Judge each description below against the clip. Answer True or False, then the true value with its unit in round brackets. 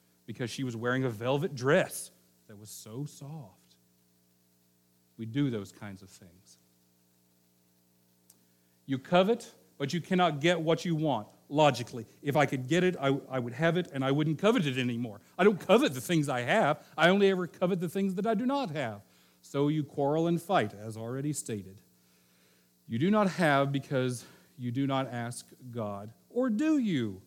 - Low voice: True (130 Hz)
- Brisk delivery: False (180 wpm)